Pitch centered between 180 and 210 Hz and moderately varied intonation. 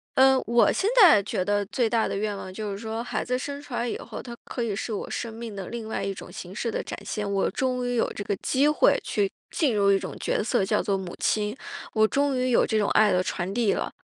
No: high, 220 Hz; average, 3.5 semitones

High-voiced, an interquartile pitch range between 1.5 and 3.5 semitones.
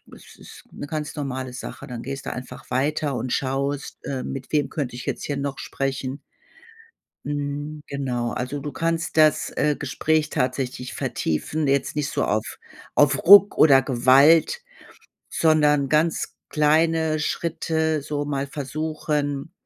No: medium, 145 Hz; narrow, 2.4 semitones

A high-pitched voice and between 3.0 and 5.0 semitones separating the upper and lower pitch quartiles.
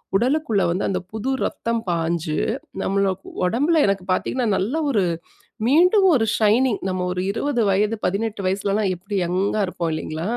Yes: high, 200 Hz; average, 4.2 semitones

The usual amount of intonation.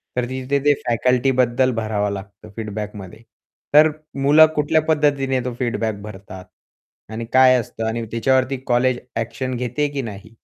Yes: average, 3.3 semitones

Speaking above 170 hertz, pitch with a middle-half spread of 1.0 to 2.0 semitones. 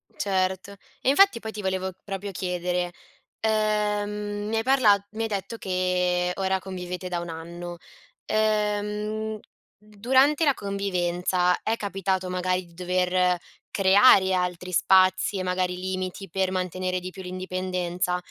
No: medium, 185 Hz; narrow, 2.4 semitones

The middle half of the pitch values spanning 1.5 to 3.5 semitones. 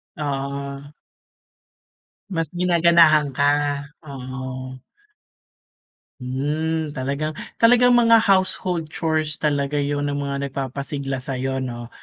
Yes: average, 3.1 semitones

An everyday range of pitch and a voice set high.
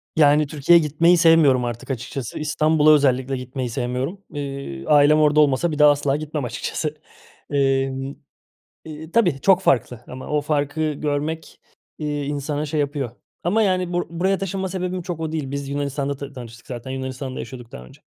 No: average, 3.0 semitones; medium, 145 Hz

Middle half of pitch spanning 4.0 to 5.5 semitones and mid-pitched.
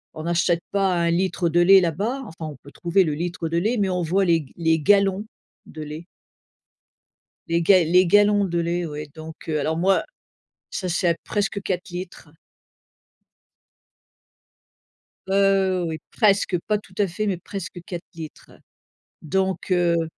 No: average, 2.7 semitones; medium, 175 Hz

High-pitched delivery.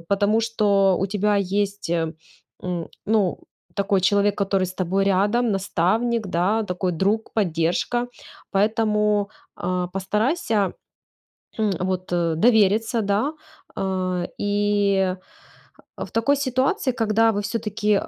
Yes: high, 205 Hz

